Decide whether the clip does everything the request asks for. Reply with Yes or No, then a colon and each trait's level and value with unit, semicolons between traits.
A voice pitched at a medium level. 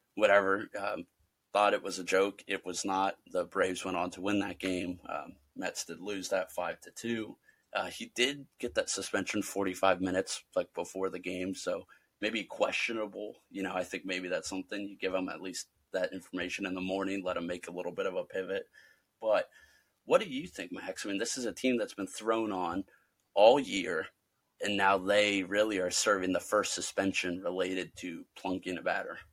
No: very low, 95 Hz